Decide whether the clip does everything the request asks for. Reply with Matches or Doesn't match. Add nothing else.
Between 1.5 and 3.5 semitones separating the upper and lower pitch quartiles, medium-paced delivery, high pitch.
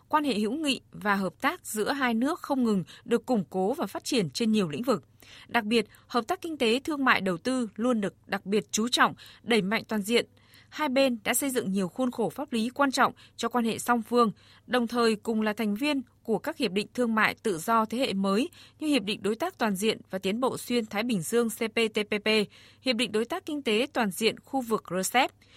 Matches